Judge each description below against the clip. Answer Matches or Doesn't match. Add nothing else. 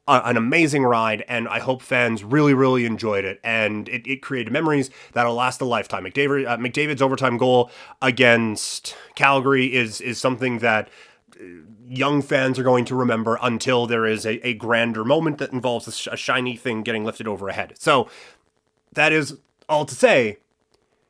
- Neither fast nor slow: Matches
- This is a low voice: Matches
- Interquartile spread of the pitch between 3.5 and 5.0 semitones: Doesn't match